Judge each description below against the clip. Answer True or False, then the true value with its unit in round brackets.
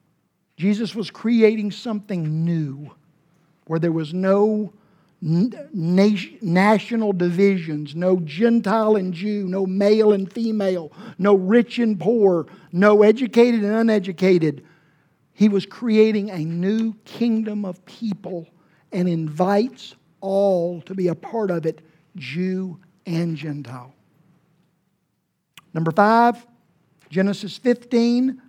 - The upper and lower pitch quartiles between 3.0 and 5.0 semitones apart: True (4.0 semitones)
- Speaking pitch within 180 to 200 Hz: True (190 Hz)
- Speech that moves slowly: True (110 wpm)